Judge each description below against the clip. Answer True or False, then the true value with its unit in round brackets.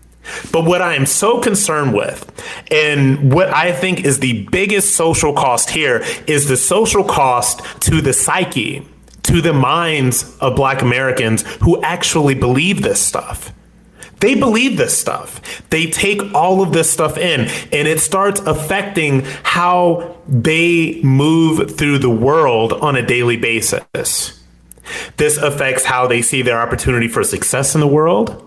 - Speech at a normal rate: True (150 wpm)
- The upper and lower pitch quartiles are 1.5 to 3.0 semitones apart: False (4.7 semitones)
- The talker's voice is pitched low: False (150 Hz)